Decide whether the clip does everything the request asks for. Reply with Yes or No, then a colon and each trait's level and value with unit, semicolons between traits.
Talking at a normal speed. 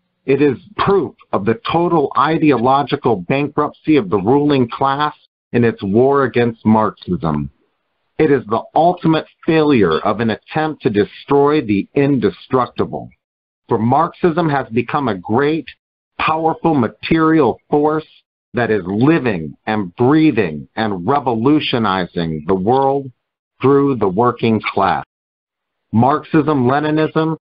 No: slow, 115 wpm